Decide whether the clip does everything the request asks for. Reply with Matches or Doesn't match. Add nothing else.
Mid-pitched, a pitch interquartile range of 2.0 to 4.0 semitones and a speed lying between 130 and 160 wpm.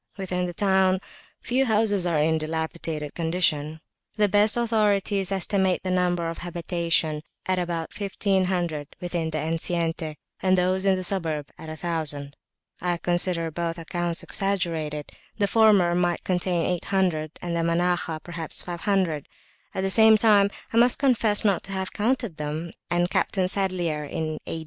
Matches